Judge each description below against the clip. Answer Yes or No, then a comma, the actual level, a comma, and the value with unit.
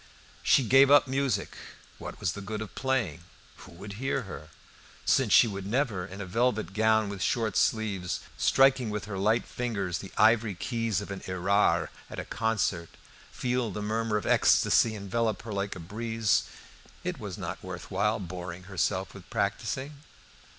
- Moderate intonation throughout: Yes, average, 3.2 semitones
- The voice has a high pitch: No, low, 105 Hz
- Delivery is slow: No, average, 170 wpm